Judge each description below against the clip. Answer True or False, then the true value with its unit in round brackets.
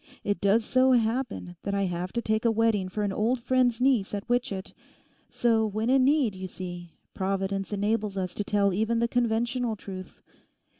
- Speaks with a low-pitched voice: False (215 Hz)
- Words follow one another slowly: False (185 wpm)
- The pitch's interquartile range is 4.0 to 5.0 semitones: False (3.4 semitones)